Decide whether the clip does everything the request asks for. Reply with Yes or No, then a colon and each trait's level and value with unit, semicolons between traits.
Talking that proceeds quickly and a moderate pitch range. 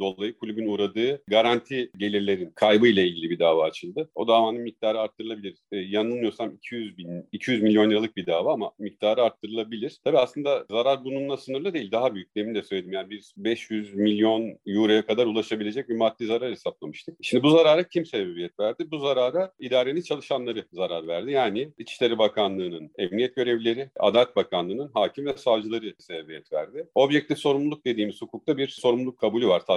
Yes: fast, 165 wpm; average, 4.1 semitones